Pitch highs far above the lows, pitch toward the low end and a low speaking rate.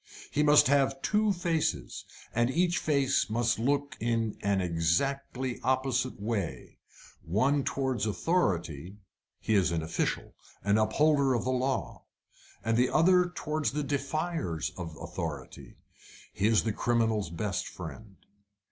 Yes: wide, 6.1 semitones; low, 120 Hz; slow, 130 wpm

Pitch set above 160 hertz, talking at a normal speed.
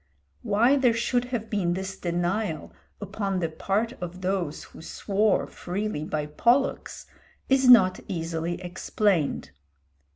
No: high, 190 Hz; slow, 125 wpm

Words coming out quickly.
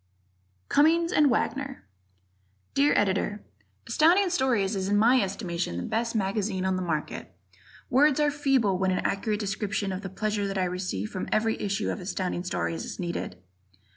No: average, 165 wpm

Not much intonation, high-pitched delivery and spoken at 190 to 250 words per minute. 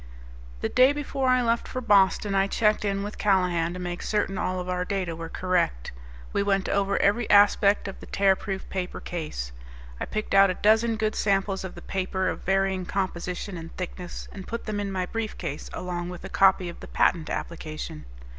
Yes: narrow, 2.3 semitones; high, 195 Hz; average, 195 wpm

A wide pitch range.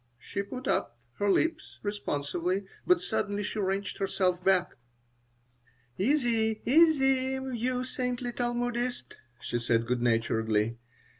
Yes: wide, 6.4 semitones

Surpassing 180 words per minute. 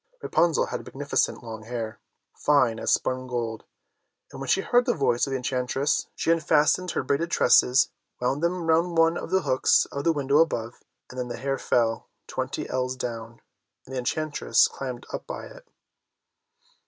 No: average, 175 wpm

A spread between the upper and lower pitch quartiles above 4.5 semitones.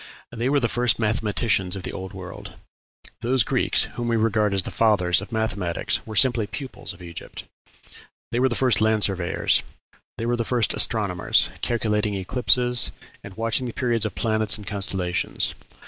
No: average, 3.3 semitones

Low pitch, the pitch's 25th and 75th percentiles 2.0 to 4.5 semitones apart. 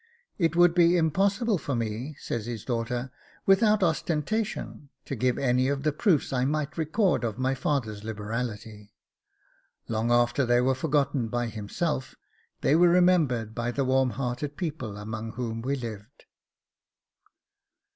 No: low, 130 Hz; average, 5.3 semitones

